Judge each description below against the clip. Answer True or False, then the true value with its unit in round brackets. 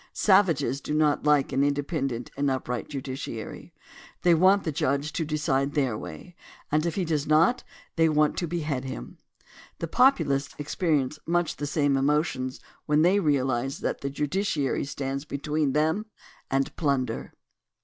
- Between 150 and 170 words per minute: True (160 wpm)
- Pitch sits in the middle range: True (145 Hz)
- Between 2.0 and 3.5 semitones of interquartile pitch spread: True (3.0 semitones)